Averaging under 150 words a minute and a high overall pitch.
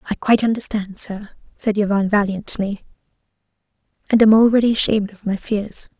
Yes: average, 140 wpm; high, 210 Hz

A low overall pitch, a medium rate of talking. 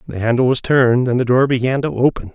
No: low, 125 Hz; fast, 255 wpm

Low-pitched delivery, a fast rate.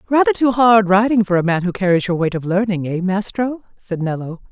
No: high, 200 Hz; fast, 225 wpm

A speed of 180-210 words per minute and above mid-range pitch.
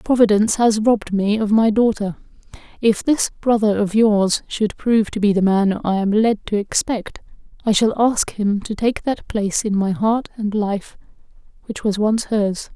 Yes: average, 190 wpm; high, 210 Hz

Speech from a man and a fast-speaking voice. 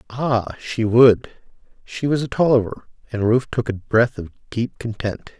No: male; average, 155 wpm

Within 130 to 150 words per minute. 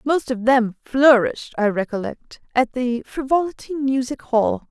Yes: average, 140 wpm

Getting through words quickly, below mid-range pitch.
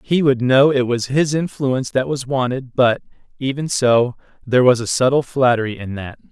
No: average, 190 wpm; low, 130 Hz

